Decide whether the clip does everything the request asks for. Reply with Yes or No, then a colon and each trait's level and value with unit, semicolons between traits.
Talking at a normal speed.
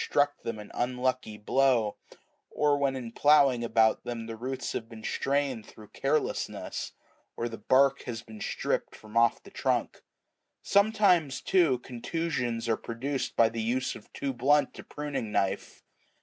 Yes: average, 155 wpm